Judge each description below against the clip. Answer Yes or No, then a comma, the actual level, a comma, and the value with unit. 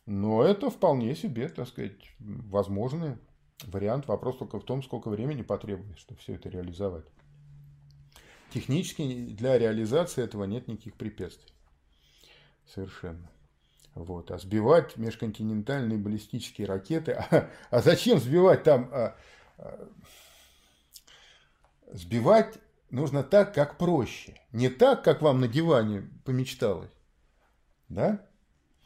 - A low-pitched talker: Yes, low, 110 Hz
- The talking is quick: No, slow, 110 wpm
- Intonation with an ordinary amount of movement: No, wide, 7.5 semitones